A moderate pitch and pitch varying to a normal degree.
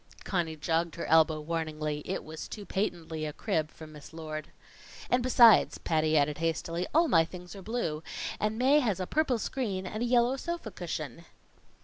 No: medium, 170 Hz; wide, 5.8 semitones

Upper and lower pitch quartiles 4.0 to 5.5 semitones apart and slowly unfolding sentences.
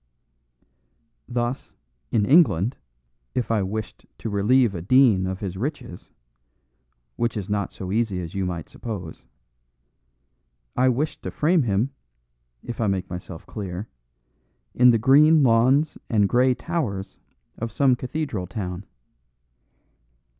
Yes: average, 5.0 semitones; slow, 125 wpm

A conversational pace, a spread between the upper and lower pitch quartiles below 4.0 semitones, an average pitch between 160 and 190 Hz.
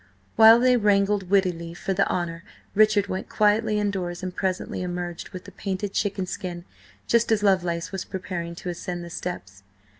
Yes: average, 170 wpm; average, 2.8 semitones; medium, 185 Hz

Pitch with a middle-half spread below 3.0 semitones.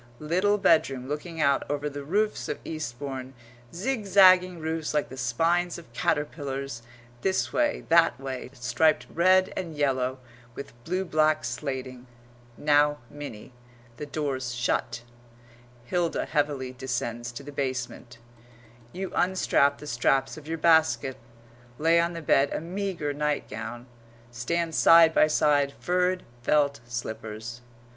No: average, 4.4 semitones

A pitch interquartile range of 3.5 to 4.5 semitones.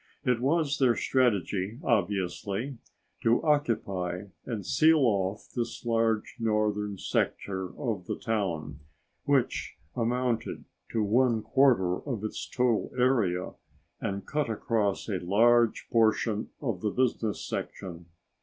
Yes: average, 3.8 semitones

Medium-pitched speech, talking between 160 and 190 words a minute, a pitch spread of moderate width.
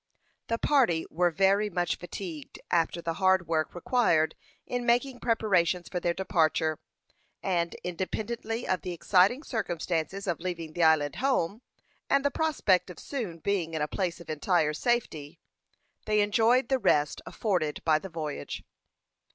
No: medium, 180 Hz; average, 150 wpm; average, 4.9 semitones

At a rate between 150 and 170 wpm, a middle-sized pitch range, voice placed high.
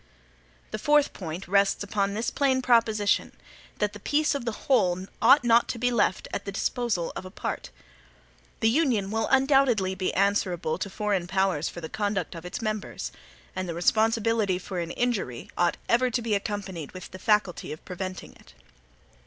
No: average, 180 wpm; average, 3.9 semitones; high, 205 Hz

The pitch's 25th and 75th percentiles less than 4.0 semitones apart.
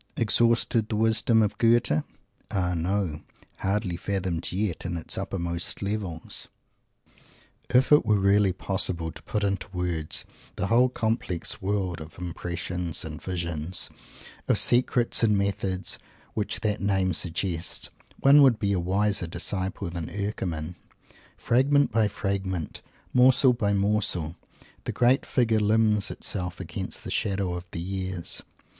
Yes: average, 3.6 semitones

